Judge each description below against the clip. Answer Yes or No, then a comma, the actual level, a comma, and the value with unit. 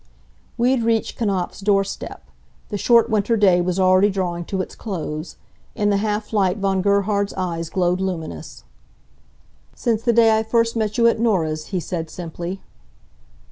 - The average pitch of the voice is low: No, high, 195 Hz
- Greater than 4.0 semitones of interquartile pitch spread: No, average, 3.5 semitones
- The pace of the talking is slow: No, average, 165 wpm